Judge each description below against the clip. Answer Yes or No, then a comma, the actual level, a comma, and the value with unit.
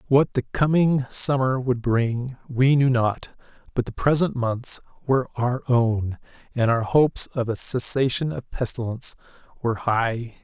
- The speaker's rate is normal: Yes, average, 150 wpm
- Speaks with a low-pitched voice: Yes, low, 125 Hz